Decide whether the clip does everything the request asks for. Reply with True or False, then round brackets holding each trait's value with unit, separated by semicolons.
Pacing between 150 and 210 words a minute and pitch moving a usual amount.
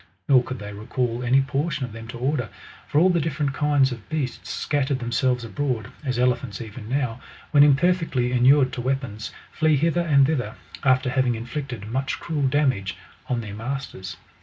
True (180 wpm; 3.2 semitones)